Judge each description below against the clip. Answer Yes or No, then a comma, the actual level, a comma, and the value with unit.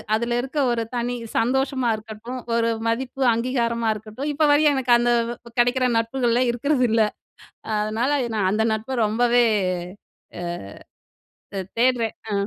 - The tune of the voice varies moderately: No, narrow, 2.2 semitones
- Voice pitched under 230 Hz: No, high, 240 Hz